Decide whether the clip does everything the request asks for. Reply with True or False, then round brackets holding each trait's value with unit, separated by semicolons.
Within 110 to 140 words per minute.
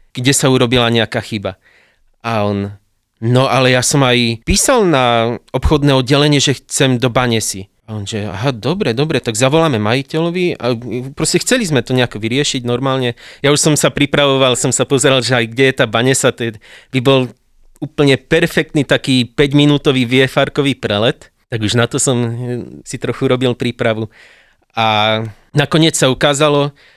False (165 wpm)